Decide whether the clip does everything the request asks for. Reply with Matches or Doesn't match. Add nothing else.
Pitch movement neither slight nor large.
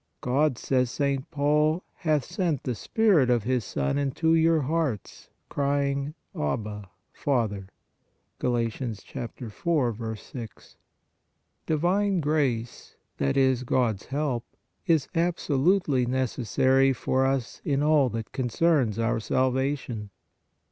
Matches